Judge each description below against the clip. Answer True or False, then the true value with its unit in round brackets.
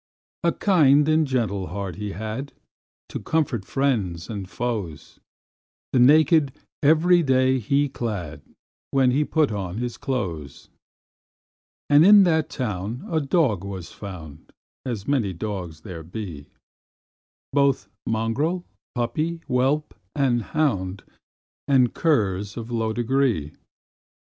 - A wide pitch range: True (6.3 semitones)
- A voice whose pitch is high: False (120 Hz)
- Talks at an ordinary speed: False (120 wpm)